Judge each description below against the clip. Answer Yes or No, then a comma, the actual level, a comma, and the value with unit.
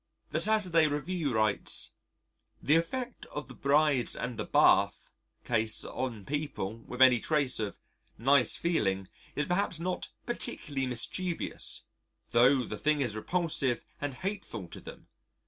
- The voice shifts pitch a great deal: Yes, wide, 5.8 semitones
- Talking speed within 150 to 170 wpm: No, slow, 135 wpm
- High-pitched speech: No, medium, 140 Hz